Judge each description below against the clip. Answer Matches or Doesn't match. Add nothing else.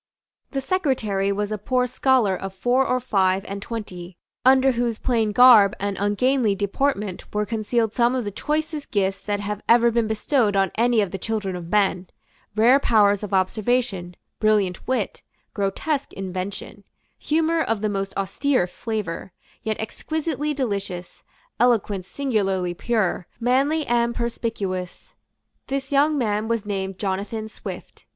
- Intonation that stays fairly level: Doesn't match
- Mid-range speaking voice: Doesn't match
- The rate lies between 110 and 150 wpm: Matches